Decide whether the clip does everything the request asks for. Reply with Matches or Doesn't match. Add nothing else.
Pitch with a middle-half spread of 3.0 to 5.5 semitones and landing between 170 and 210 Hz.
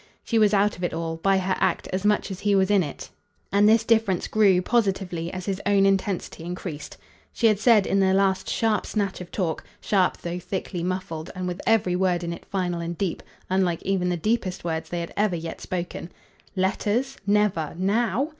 Doesn't match